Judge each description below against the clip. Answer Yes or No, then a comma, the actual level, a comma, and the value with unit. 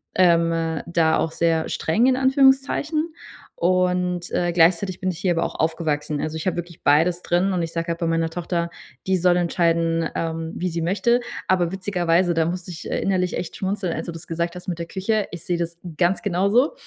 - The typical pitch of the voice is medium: Yes, medium, 175 Hz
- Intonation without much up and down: Yes, narrow, 2.0 semitones